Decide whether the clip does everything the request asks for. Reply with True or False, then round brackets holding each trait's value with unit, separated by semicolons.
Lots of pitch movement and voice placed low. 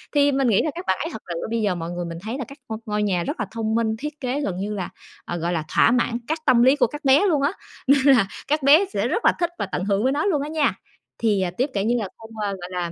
False (6.2 semitones; 230 Hz)